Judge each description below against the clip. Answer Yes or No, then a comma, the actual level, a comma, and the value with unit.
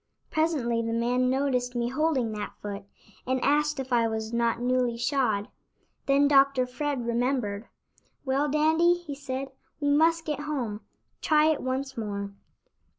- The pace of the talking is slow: No, average, 150 wpm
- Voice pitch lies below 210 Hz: No, very high, 260 Hz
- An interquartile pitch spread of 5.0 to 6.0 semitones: No, average, 3.8 semitones